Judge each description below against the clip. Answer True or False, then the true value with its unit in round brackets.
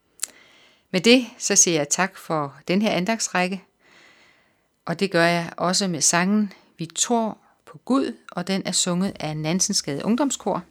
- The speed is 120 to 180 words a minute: True (155 wpm)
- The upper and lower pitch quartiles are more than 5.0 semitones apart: False (3.2 semitones)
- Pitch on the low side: False (185 Hz)